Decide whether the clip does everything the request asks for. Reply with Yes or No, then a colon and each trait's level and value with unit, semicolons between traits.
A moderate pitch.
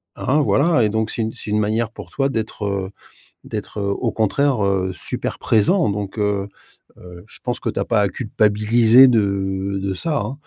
No: low, 105 Hz